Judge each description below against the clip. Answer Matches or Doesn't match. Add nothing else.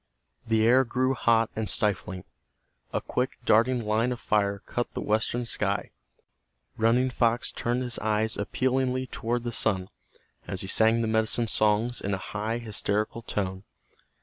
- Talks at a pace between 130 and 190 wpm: Matches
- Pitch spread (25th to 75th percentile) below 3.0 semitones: Matches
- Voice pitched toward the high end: Doesn't match